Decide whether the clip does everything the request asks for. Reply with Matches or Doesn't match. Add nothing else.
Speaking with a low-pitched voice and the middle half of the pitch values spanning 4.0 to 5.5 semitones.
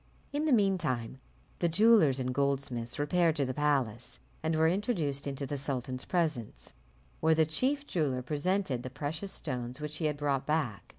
Doesn't match